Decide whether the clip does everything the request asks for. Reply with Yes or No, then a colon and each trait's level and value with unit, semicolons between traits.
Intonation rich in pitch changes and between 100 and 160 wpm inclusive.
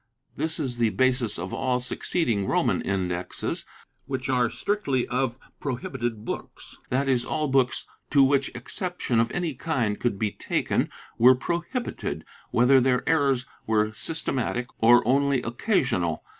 No: average, 3.1 semitones; average, 150 wpm